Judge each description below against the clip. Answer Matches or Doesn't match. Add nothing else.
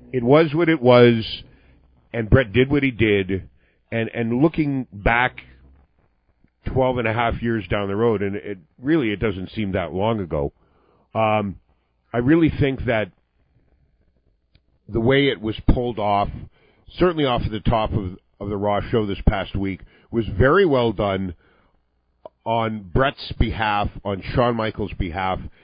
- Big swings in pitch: Doesn't match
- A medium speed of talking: Matches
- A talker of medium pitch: Doesn't match